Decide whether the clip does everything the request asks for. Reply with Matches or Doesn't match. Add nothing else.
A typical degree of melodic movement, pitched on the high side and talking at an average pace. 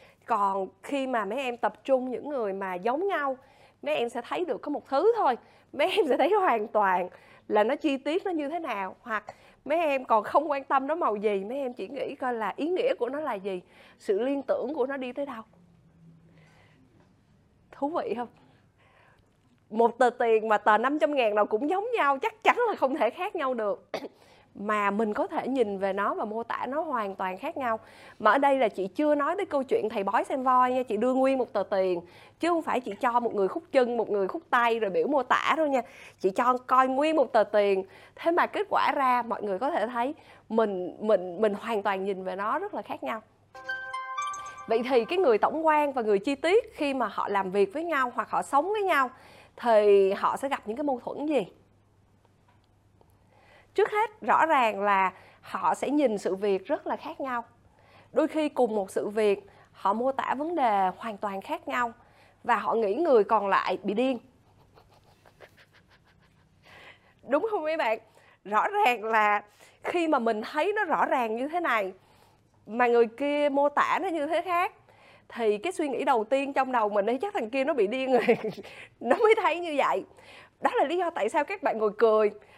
Doesn't match